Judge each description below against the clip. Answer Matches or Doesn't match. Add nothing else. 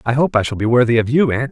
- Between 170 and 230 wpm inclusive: Doesn't match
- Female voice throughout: Doesn't match